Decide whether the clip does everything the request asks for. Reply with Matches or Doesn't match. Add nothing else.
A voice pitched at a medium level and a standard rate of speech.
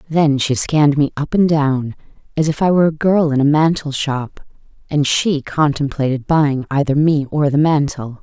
Matches